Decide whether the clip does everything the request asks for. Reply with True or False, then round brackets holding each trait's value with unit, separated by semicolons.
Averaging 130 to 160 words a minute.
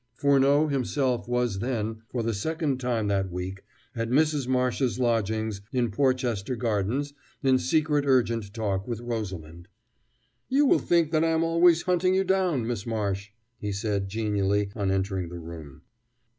True (155 wpm)